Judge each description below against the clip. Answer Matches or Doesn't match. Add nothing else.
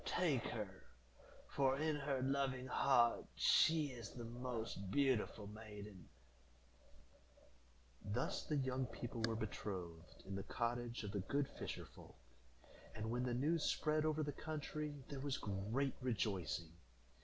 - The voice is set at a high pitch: Doesn't match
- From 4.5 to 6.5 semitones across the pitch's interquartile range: Matches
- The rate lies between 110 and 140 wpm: Matches